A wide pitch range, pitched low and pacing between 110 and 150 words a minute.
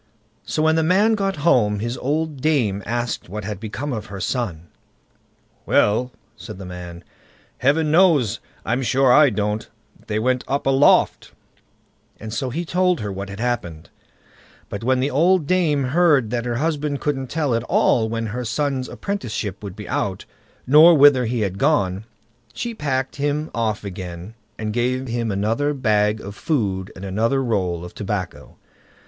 No: wide, 5.7 semitones; low, 120 Hz; average, 165 wpm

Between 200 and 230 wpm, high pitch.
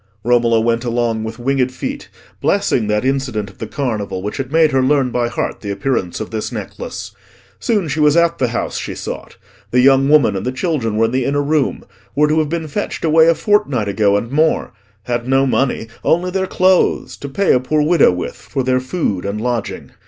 No: fast, 205 wpm; low, 130 Hz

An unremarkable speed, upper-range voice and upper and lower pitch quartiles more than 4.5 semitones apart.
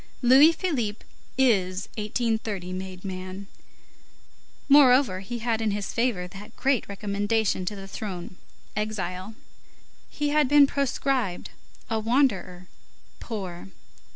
No: slow, 110 wpm; high, 215 Hz; average, 4.9 semitones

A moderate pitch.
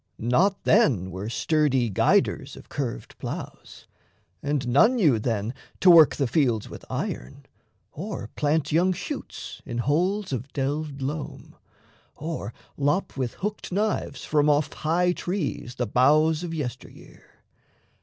Yes: medium, 145 Hz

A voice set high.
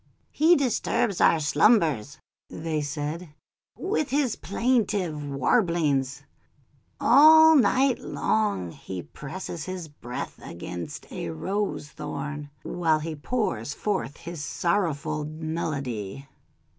No: medium, 160 Hz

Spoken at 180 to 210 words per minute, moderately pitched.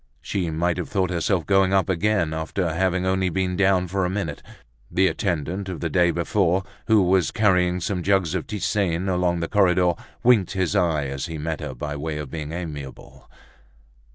No: average, 185 wpm; very low, 90 Hz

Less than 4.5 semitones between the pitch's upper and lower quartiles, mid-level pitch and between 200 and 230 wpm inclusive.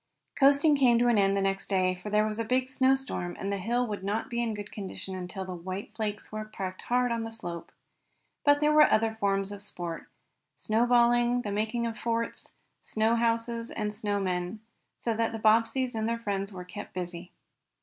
No: average, 3.2 semitones; high, 215 Hz; fast, 205 wpm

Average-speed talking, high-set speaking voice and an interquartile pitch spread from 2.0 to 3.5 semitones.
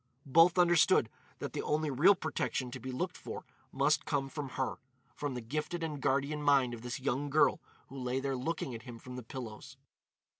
No: average, 190 wpm; low, 135 Hz; average, 3.1 semitones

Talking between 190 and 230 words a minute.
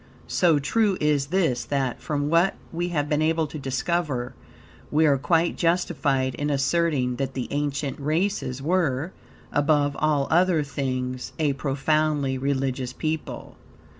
No: slow, 135 wpm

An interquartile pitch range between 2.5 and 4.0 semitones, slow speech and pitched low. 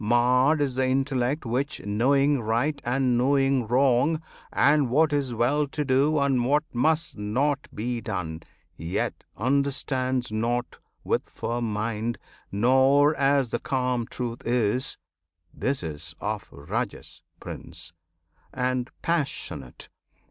Yes: average, 3.2 semitones; slow, 120 wpm; low, 125 Hz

